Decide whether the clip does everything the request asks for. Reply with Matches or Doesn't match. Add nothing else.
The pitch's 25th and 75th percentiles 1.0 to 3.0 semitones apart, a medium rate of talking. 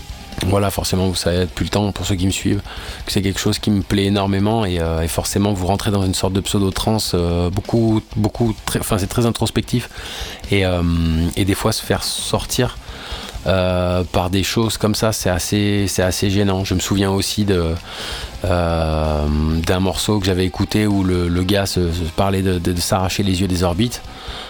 Matches